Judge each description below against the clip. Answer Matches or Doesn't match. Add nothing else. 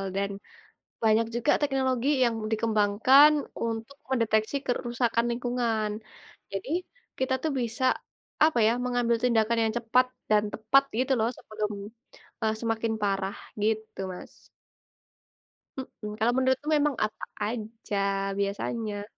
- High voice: Matches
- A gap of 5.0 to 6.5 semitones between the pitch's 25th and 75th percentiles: Doesn't match